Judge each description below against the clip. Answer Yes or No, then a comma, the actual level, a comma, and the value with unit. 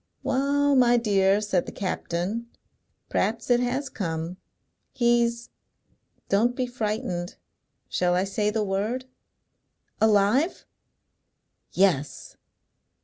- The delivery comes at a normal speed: No, slow, 100 wpm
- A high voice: Yes, high, 220 Hz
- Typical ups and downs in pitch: Yes, average, 4.1 semitones